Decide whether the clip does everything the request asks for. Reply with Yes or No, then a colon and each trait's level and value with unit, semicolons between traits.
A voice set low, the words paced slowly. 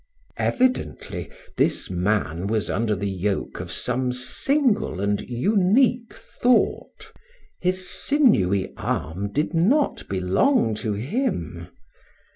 Yes: low, 125 Hz; slow, 100 wpm